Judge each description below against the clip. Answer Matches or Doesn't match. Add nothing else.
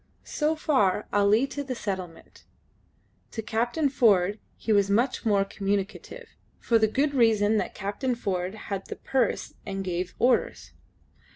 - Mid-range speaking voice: Doesn't match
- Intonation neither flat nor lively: Matches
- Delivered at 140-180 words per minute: Matches